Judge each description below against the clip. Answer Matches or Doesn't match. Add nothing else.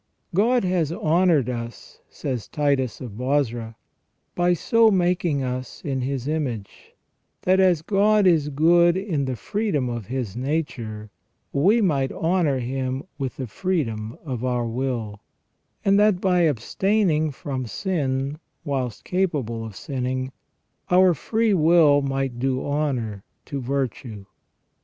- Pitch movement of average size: Doesn't match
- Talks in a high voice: Doesn't match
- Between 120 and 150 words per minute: Matches